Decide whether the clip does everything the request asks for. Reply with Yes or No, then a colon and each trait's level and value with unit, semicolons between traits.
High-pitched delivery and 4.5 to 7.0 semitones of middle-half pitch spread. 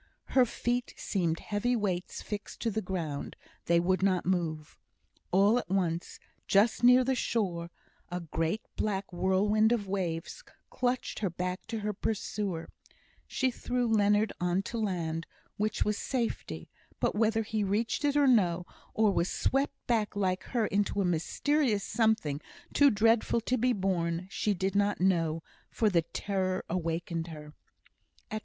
No: high, 200 Hz; average, 4.1 semitones